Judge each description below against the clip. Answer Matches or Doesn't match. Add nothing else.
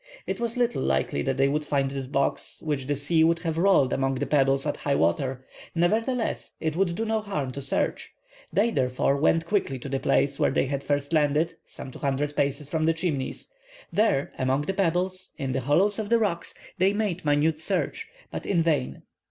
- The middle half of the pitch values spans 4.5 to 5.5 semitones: Matches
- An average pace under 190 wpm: Doesn't match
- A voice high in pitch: Doesn't match